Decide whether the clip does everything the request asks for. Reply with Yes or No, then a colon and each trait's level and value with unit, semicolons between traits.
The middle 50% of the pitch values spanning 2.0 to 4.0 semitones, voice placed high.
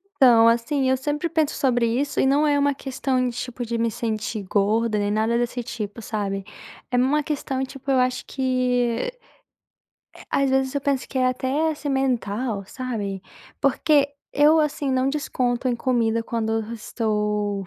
Yes: average, 3.2 semitones; very high, 255 Hz